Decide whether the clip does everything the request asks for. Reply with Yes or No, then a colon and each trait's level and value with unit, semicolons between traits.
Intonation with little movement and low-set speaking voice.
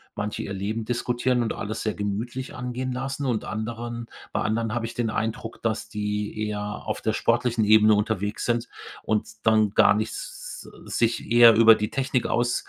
Yes: narrow, 2.0 semitones; low, 115 Hz